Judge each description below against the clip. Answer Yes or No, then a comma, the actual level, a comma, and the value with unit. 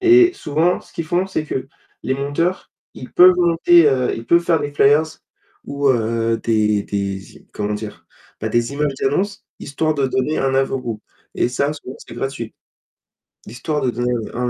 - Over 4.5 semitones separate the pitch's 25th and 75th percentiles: Yes, average, 5.0 semitones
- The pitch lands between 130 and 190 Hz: Yes, low, 135 Hz